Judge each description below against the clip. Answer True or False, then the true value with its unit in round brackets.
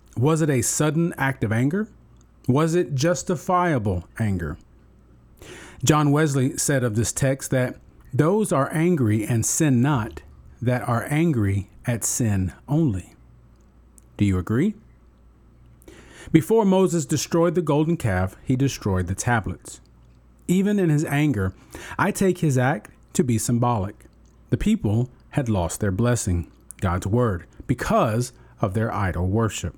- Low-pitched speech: True (120 Hz)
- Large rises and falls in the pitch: True (7.7 semitones)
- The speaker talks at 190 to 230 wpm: False (135 wpm)